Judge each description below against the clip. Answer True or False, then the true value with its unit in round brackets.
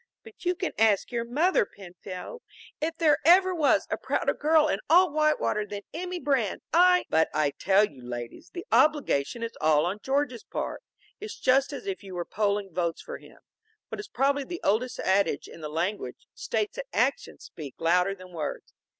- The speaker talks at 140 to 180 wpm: False (190 wpm)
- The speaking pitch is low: False (230 Hz)